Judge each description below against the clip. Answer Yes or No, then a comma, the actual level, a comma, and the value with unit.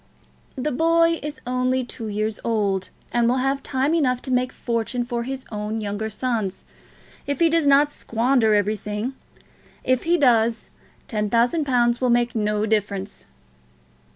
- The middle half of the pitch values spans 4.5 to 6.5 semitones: No, average, 3.7 semitones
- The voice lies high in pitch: Yes, high, 240 Hz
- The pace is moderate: Yes, average, 155 wpm